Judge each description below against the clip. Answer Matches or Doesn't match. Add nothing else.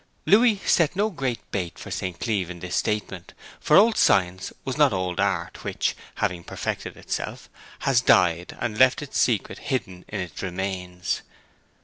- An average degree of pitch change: Doesn't match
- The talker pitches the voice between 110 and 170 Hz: Doesn't match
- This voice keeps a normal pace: Matches